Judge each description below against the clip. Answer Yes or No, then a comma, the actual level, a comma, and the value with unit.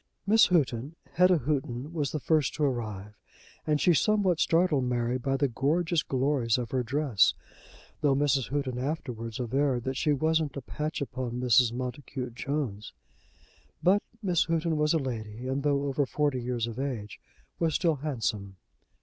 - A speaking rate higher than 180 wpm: No, average, 160 wpm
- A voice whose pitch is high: No, low, 135 Hz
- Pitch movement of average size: Yes, average, 3.8 semitones